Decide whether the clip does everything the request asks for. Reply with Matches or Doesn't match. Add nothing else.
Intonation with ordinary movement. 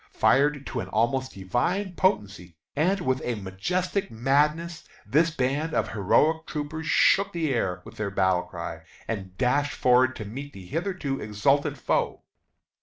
Doesn't match